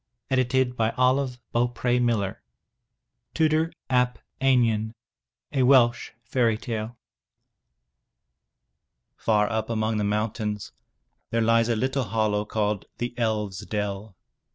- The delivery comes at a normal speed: No, slow, 105 wpm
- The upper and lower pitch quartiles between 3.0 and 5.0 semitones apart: No, narrow, 2.6 semitones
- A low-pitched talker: Yes, low, 115 Hz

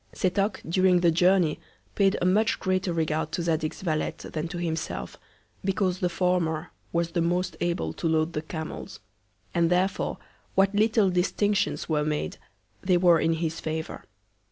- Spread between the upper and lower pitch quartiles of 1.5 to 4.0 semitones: Yes, narrow, 2.6 semitones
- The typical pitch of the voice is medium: Yes, medium, 175 Hz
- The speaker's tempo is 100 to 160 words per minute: Yes, average, 155 wpm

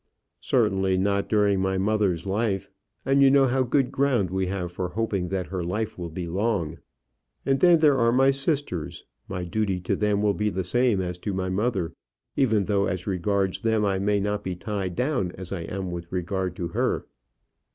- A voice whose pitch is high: No, low, 100 Hz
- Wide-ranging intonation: No, average, 3.4 semitones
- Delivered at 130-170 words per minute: No, average, 195 wpm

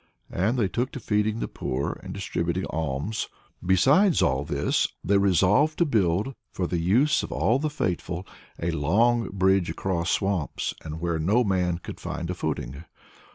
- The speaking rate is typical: Yes, average, 165 wpm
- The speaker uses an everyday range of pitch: Yes, average, 5.0 semitones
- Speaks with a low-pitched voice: Yes, very low, 95 Hz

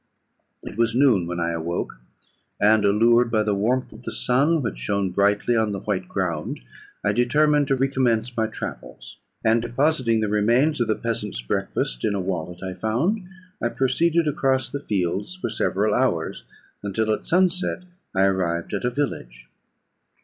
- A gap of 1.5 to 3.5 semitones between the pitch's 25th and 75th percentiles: No, average, 5.2 semitones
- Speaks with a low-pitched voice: Yes, low, 110 Hz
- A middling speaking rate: Yes, average, 165 wpm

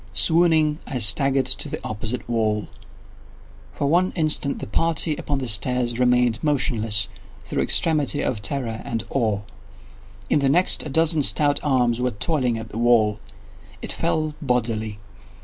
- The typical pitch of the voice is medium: No, low, 125 Hz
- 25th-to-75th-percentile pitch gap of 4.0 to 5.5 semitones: Yes, average, 4.9 semitones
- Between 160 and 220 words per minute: No, average, 150 wpm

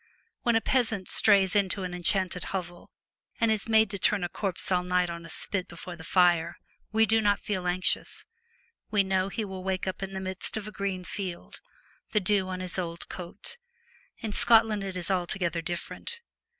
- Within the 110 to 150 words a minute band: No, average, 190 wpm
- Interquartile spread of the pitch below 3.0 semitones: Yes, narrow, 2.6 semitones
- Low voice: No, high, 190 Hz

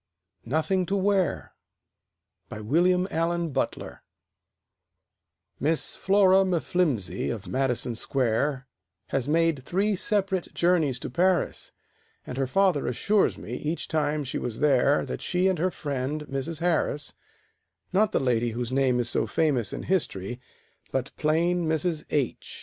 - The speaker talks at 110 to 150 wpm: Yes, slow, 135 wpm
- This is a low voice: No, medium, 155 Hz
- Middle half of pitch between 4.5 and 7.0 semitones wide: Yes, wide, 5.6 semitones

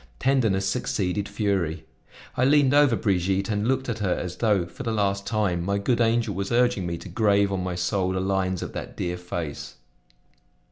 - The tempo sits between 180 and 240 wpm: Yes, average, 190 wpm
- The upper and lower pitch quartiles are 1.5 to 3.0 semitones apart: No, average, 3.8 semitones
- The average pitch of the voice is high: No, low, 100 Hz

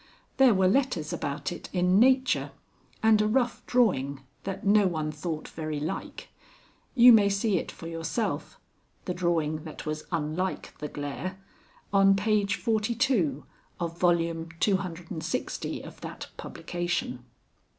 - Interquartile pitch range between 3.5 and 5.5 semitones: Yes, average, 5.1 semitones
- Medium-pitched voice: Yes, medium, 180 Hz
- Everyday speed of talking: No, slow, 130 wpm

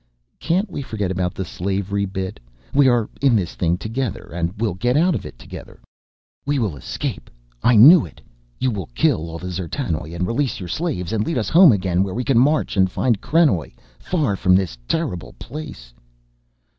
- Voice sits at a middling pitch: No, low, 105 Hz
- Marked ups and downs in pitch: Yes, wide, 7.1 semitones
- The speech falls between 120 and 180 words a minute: No, average, 190 wpm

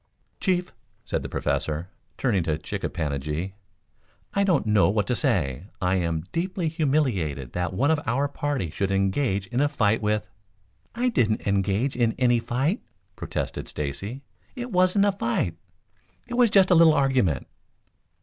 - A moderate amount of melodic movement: No, wide, 9.0 semitones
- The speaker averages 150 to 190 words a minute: Yes, average, 170 wpm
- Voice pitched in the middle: No, low, 115 Hz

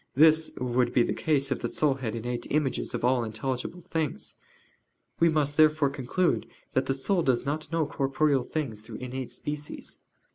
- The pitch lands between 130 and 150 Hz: Yes, medium, 140 Hz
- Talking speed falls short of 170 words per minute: No, average, 180 wpm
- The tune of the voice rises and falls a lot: No, average, 3.4 semitones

